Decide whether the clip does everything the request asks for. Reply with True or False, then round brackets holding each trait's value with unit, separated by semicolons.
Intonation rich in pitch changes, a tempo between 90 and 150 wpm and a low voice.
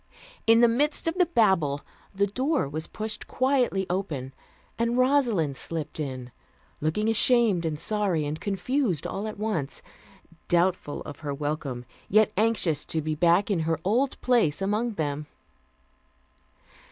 False (6.8 semitones; 140 wpm; 195 Hz)